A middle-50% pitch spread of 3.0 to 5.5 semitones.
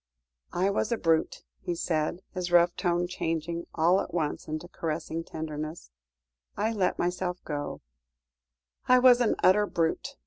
No: narrow, 2.4 semitones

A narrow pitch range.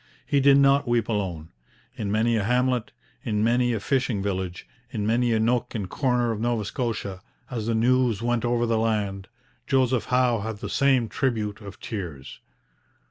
No: average, 3.1 semitones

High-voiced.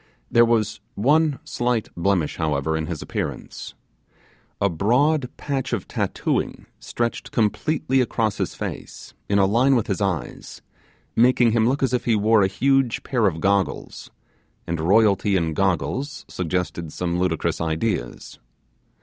No: low, 105 Hz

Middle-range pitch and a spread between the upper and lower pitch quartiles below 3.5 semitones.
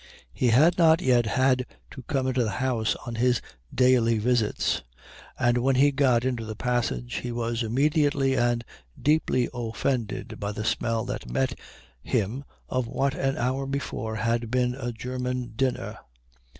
No: low, 125 Hz; narrow, 2.4 semitones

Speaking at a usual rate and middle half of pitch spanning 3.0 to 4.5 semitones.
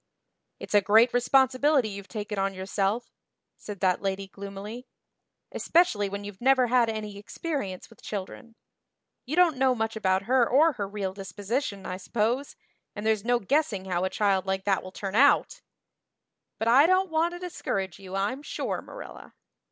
No: average, 165 wpm; average, 4.9 semitones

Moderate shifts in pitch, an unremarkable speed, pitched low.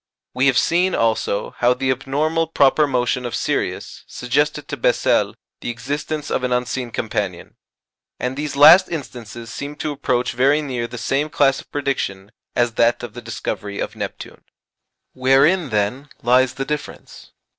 Yes: average, 3.4 semitones; average, 155 wpm; low, 130 Hz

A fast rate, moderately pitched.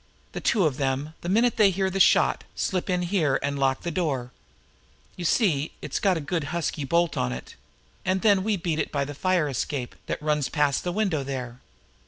Yes: fast, 210 wpm; medium, 160 Hz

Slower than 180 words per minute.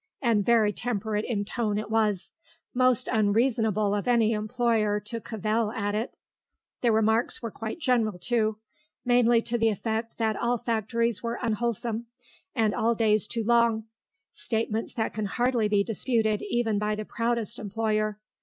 Yes: average, 155 wpm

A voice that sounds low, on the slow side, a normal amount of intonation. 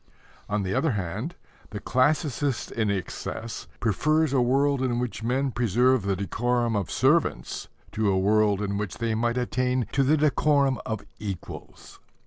No: low, 120 Hz; average, 155 wpm; average, 4.2 semitones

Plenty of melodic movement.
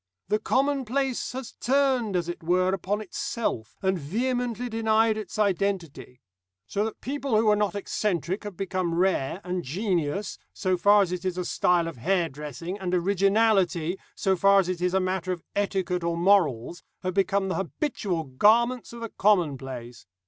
No: average, 3.8 semitones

